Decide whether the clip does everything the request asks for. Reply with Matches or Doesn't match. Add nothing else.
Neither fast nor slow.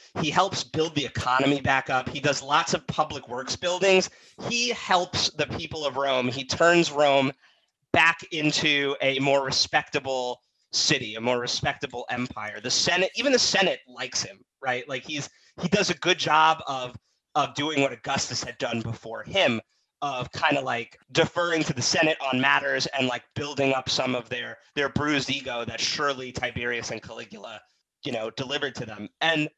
Matches